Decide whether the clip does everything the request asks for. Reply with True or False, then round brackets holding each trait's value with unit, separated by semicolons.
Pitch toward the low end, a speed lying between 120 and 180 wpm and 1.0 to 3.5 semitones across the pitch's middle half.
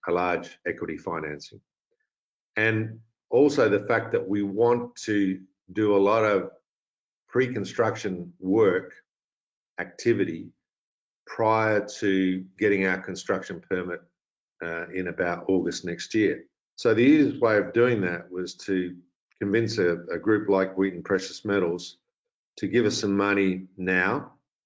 True (95 Hz; 135 wpm; 3.0 semitones)